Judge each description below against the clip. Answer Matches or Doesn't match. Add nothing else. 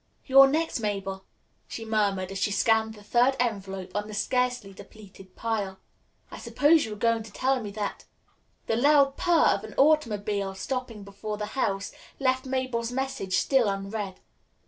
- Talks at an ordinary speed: Matches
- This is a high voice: Matches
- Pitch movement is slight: Doesn't match